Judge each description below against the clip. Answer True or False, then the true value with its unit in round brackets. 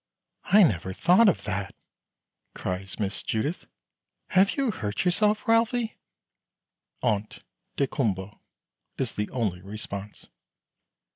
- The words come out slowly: True (100 wpm)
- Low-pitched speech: True (110 Hz)